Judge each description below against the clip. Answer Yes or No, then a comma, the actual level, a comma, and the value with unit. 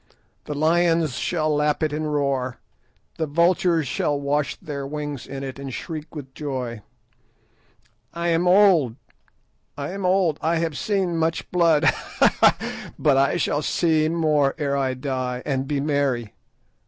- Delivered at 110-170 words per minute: Yes, average, 155 wpm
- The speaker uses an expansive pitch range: No, average, 3.1 semitones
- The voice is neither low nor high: Yes, medium, 150 Hz